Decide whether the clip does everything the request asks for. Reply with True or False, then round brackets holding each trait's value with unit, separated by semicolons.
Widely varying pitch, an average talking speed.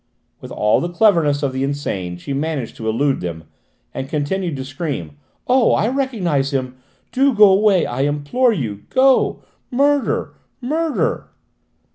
True (8.9 semitones; 145 wpm)